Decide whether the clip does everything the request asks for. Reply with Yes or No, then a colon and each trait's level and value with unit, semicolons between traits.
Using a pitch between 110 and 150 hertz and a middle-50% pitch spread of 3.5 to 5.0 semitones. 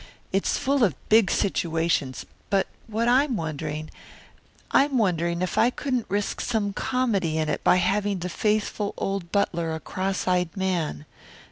No: high, 195 Hz; average, 4.2 semitones